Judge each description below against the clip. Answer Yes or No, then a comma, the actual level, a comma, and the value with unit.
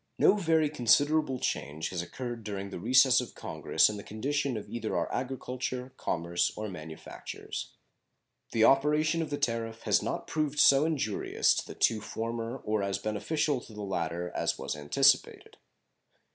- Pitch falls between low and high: No, low, 120 Hz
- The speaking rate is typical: Yes, average, 160 wpm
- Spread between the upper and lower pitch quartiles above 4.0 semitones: Yes, average, 5.3 semitones